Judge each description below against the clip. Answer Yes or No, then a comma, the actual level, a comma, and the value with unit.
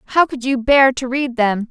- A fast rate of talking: Yes, fast, 245 wpm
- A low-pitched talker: No, very high, 255 Hz